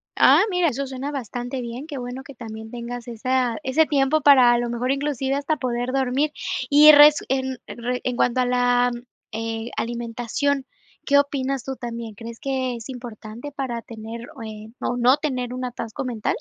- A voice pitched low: No, very high, 250 Hz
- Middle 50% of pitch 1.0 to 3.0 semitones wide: Yes, narrow, 2.5 semitones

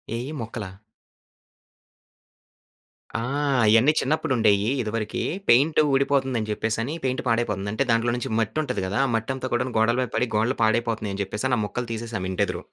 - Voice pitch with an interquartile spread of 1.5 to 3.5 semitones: Yes, average, 2.9 semitones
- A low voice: Yes, low, 115 Hz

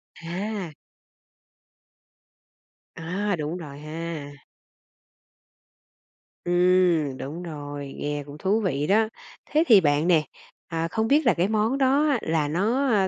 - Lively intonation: Yes, wide, 5.7 semitones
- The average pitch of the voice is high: No, medium, 175 Hz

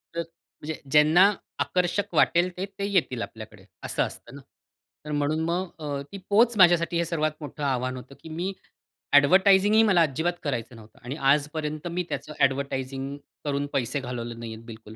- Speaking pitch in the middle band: Yes, medium, 150 Hz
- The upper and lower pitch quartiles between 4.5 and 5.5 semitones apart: Yes, average, 4.9 semitones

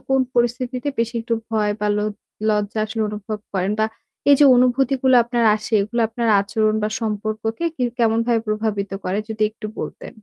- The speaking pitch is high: Yes, high, 220 Hz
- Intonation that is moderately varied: No, narrow, 2.1 semitones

